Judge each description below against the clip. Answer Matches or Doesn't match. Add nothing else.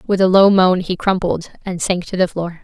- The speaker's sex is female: Matches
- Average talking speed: Doesn't match